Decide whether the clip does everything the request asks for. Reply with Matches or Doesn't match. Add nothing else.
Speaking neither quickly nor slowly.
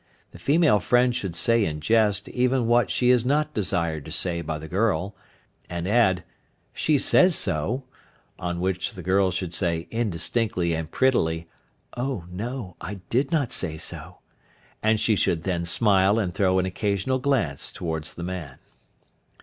Matches